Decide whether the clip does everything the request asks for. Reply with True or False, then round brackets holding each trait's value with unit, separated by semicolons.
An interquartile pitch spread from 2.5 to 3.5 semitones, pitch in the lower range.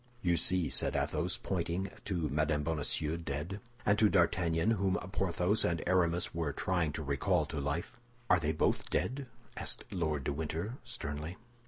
True (3.2 semitones; 85 Hz)